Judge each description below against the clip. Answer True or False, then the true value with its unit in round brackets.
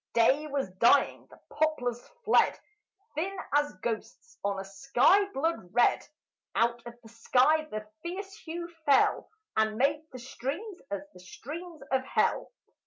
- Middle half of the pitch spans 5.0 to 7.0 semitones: True (5.3 semitones)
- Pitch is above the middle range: True (275 Hz)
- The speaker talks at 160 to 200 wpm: False (145 wpm)